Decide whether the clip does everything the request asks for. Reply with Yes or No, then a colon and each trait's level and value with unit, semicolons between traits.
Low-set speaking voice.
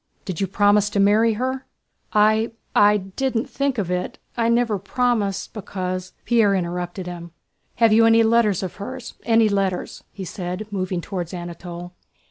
No: high, 205 Hz